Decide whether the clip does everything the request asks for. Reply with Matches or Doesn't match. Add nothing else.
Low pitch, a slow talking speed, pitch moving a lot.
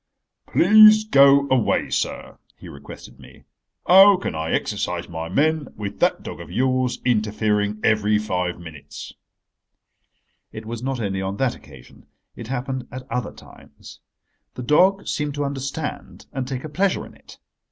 Doesn't match